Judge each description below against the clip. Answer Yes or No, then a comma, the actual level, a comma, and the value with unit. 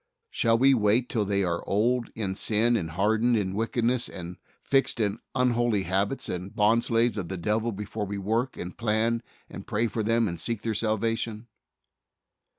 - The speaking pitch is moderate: No, low, 110 Hz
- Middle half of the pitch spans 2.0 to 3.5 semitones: Yes, average, 2.8 semitones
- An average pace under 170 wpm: No, average, 180 wpm